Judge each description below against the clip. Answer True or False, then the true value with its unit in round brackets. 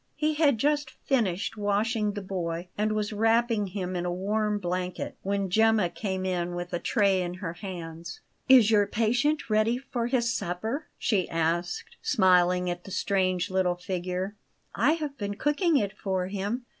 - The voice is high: True (200 Hz)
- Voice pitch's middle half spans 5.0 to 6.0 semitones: False (3.8 semitones)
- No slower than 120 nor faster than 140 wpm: False (170 wpm)